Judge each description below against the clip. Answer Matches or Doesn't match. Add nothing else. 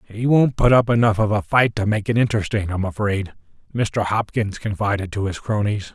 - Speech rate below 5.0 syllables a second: Doesn't match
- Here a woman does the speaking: Doesn't match